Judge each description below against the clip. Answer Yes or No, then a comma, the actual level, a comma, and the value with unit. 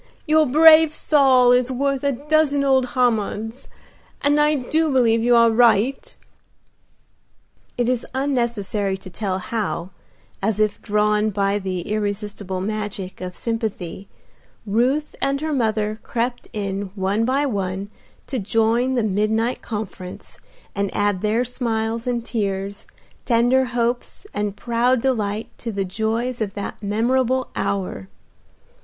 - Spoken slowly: Yes, slow, 130 wpm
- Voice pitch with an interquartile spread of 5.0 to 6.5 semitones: No, average, 3.9 semitones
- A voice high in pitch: Yes, high, 225 Hz